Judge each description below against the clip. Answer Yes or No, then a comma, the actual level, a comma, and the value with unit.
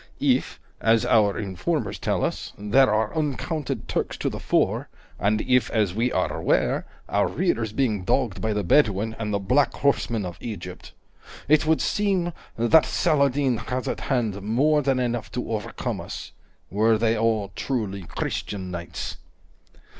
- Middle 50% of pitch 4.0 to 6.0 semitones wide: Yes, average, 4.5 semitones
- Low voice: Yes, low, 115 Hz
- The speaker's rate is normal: Yes, average, 160 wpm